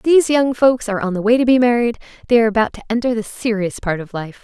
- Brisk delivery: Yes, fast, 270 wpm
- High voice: Yes, high, 230 Hz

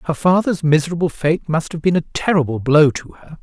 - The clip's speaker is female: No, male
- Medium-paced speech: No, fast, 210 wpm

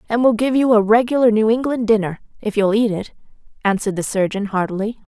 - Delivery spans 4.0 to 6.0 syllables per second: No, 6.3 syllables/s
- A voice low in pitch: No, high, 220 Hz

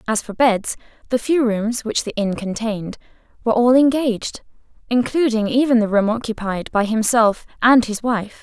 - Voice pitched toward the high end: Yes, high, 230 Hz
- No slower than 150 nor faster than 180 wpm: Yes, average, 165 wpm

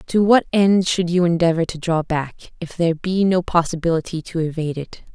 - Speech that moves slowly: No, average, 200 wpm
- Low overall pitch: No, medium, 170 Hz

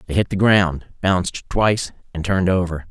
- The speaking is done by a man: Yes, male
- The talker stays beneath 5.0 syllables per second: No, 5.4 syllables/s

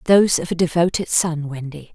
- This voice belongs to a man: No, female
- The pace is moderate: Yes, average, 185 wpm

